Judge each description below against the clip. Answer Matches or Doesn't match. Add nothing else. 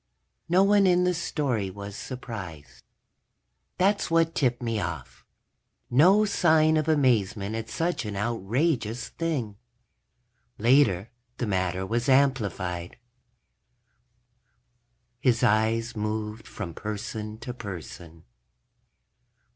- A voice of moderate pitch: Doesn't match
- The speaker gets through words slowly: Matches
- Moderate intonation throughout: Doesn't match